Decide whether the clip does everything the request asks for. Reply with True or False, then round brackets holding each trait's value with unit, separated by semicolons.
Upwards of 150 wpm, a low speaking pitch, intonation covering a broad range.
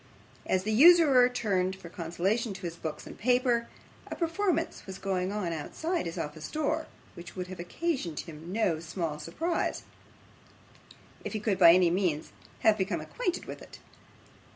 False (160 wpm; 190 Hz; 6.6 semitones)